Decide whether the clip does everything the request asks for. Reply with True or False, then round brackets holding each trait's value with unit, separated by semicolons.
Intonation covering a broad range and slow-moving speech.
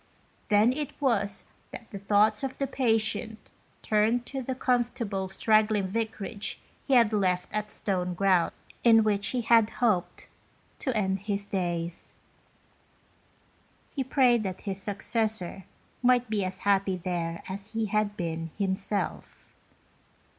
False (3.2 semitones; 130 wpm)